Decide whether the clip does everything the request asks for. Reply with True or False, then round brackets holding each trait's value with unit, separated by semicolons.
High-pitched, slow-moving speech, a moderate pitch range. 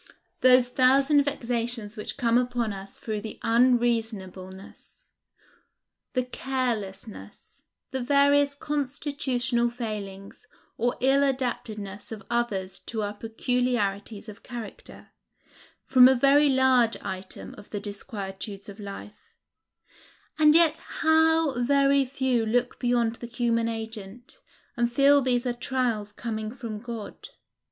True (240 Hz; 115 wpm; 3.5 semitones)